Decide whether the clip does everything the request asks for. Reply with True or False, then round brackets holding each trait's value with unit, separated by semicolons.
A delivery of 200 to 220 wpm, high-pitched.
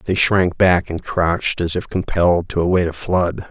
False (205 wpm; 90 Hz)